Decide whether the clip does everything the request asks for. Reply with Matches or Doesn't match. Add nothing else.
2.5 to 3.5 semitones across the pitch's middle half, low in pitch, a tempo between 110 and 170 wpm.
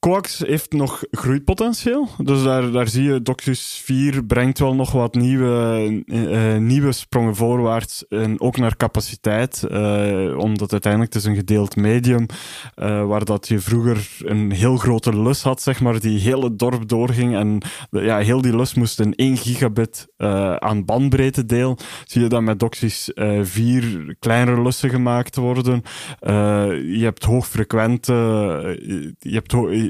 Matches